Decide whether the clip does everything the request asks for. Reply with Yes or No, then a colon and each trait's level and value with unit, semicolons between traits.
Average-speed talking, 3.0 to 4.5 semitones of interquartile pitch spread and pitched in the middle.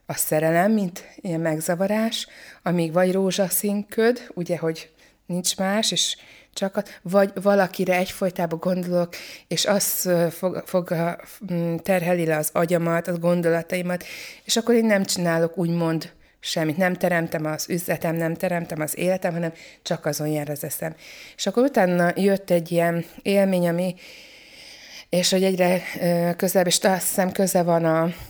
No: average, 140 wpm; narrow, 2.4 semitones; medium, 180 Hz